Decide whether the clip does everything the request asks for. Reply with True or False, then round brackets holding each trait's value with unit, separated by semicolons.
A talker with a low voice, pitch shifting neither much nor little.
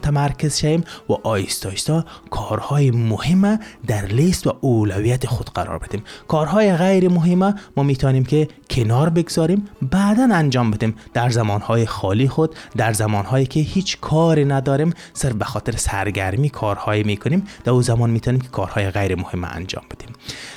False (125 Hz; 6.5 semitones)